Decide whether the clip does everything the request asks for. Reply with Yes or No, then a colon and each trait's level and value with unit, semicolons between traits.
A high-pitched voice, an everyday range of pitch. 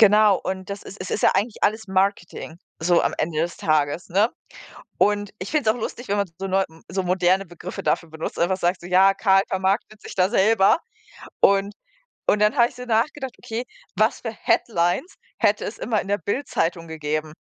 Yes: high, 195 Hz; average, 3.2 semitones